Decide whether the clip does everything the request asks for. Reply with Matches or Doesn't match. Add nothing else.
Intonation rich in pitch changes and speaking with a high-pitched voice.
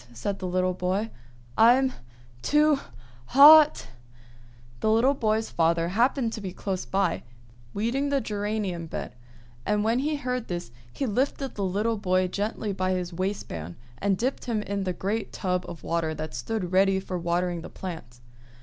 Doesn't match